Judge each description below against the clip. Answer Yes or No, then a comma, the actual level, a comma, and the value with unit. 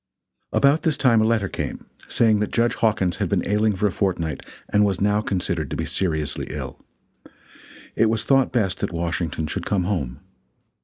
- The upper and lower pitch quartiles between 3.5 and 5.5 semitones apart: Yes, average, 4.2 semitones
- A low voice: Yes, low, 100 Hz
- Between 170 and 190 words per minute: Yes, average, 185 wpm